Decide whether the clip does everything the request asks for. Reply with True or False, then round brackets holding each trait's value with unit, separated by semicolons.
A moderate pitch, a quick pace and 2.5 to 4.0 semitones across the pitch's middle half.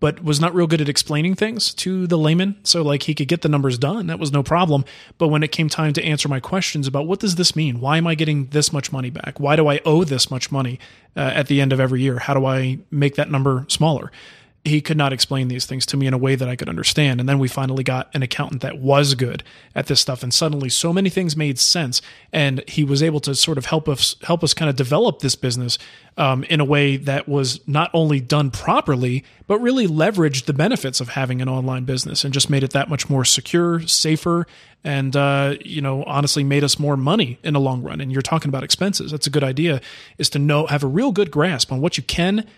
True (145 Hz; 255 wpm; 2.9 semitones)